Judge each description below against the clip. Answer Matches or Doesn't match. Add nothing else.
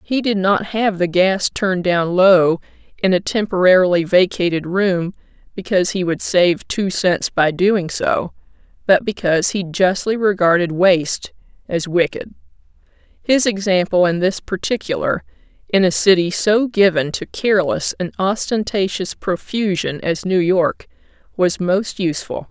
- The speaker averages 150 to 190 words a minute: Doesn't match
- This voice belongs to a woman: Matches